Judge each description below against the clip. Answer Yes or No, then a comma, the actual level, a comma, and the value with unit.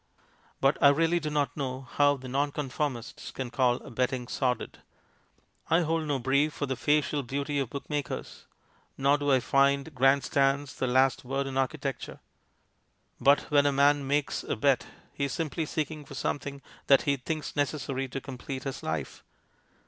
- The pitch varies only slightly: Yes, narrow, 1.6 semitones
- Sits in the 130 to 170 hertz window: Yes, medium, 140 Hz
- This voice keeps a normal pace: Yes, average, 170 wpm